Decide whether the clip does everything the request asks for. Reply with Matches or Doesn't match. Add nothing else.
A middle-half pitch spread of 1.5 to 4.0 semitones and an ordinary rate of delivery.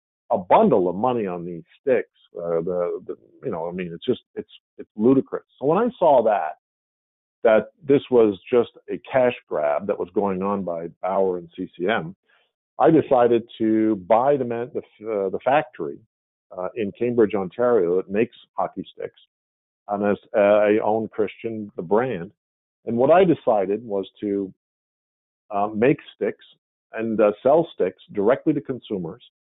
Doesn't match